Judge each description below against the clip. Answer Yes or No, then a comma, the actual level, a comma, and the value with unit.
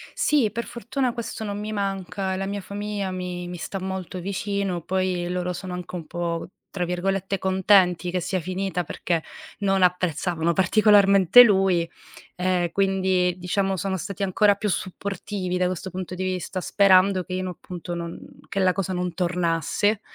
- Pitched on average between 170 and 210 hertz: Yes, medium, 185 Hz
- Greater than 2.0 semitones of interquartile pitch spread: No, narrow, 1.7 semitones